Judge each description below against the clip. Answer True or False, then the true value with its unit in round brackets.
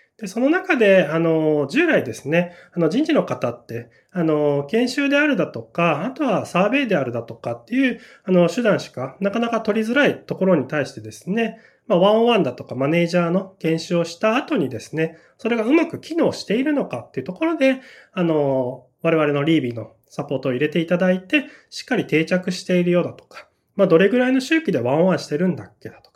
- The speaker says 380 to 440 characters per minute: True (420 characters per minute)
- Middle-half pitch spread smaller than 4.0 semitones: False (7.4 semitones)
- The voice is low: False (180 Hz)